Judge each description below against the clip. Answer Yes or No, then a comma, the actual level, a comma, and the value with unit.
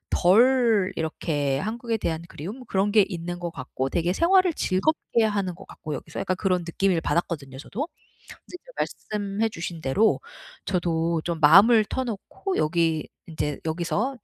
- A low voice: No, medium, 185 Hz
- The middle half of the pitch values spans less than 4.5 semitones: No, average, 5.2 semitones